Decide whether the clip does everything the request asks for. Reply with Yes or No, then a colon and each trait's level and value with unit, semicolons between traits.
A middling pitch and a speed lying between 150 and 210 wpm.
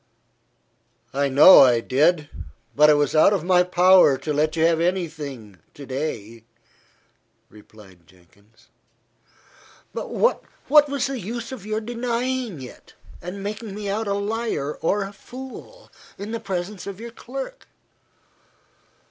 No: medium, 180 Hz; average, 140 wpm